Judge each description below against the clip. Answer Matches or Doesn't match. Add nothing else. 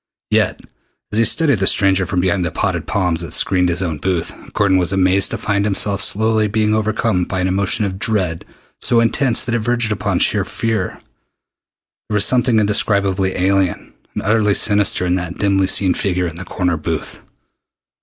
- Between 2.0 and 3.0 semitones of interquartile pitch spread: Matches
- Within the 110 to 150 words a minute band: Doesn't match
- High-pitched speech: Doesn't match